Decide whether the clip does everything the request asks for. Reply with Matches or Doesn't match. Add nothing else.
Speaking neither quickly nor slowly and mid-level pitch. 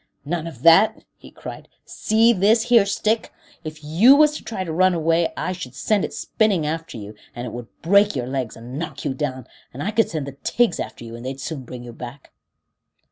Doesn't match